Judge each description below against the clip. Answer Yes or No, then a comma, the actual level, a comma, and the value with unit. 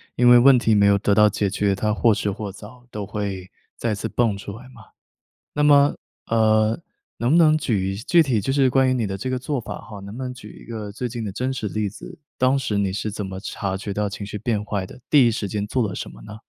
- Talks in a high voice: No, low, 110 Hz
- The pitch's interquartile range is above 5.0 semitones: No, average, 3.7 semitones